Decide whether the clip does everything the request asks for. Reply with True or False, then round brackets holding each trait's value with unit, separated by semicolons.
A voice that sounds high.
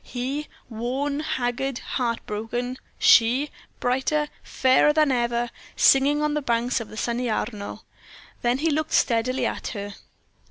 True (250 Hz)